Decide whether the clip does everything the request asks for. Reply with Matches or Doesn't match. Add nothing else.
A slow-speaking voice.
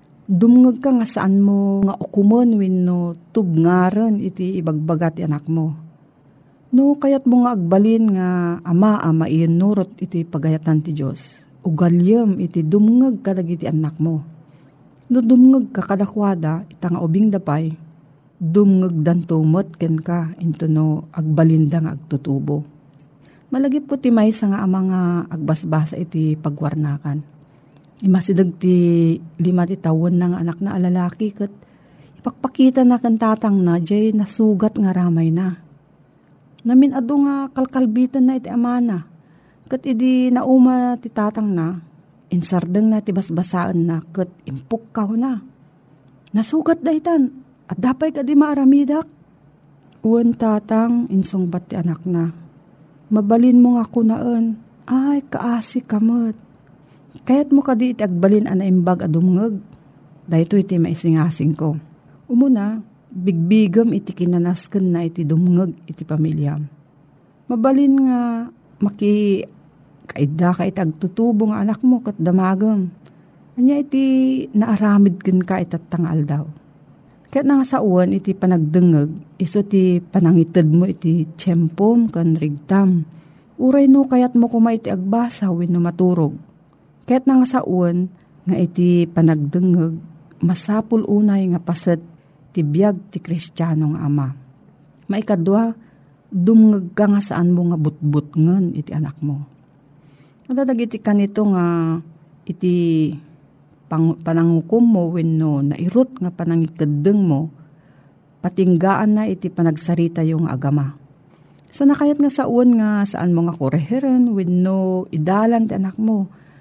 Doesn't match